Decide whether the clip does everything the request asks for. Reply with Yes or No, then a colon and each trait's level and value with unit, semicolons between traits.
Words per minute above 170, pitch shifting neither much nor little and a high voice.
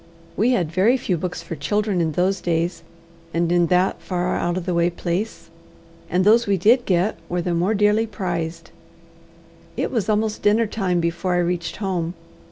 No: average, 180 wpm; average, 3.3 semitones; medium, 180 Hz